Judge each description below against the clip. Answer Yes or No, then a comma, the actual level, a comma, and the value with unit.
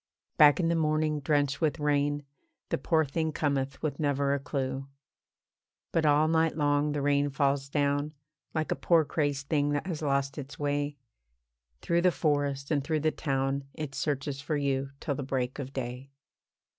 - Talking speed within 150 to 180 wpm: Yes, average, 175 wpm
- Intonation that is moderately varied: No, narrow, 1.8 semitones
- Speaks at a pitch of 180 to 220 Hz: No, medium, 145 Hz